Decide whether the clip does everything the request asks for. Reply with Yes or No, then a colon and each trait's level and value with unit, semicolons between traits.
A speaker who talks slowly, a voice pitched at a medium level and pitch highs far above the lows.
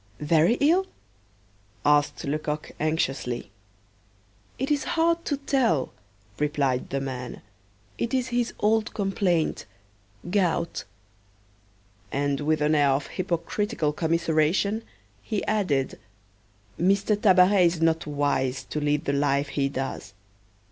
Yes: slow, 115 wpm; medium, 160 Hz; wide, 6.3 semitones